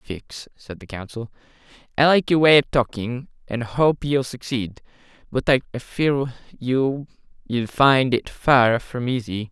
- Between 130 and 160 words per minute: Yes, average, 150 wpm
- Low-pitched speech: Yes, low, 125 Hz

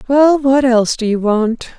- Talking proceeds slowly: No, average, 200 wpm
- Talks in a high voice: Yes, very high, 250 Hz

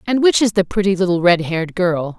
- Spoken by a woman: Yes, female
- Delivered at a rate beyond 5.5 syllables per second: Yes, 5.9 syllables/s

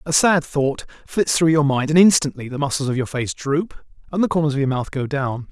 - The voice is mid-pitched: Yes, medium, 145 Hz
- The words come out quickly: Yes, fast, 250 wpm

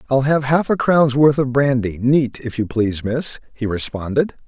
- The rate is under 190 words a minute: No, average, 200 wpm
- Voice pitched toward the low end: Yes, low, 130 Hz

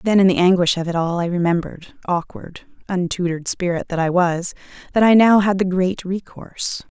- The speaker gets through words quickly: No, average, 190 wpm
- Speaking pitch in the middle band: Yes, medium, 180 Hz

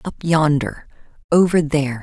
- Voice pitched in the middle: Yes, medium, 155 Hz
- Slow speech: Yes, slow, 120 wpm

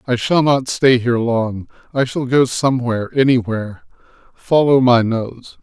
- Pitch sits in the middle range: No, low, 125 Hz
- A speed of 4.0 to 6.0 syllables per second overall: Yes, 4.6 syllables/s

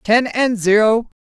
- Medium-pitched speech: No, high, 225 Hz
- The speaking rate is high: No, average, 145 wpm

